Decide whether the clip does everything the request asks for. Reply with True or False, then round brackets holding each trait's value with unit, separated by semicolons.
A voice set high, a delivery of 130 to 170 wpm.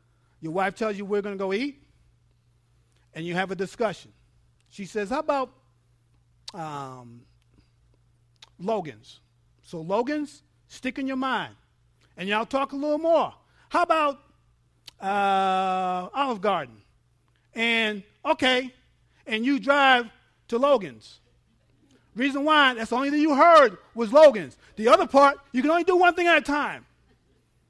True (205 Hz; 140 wpm)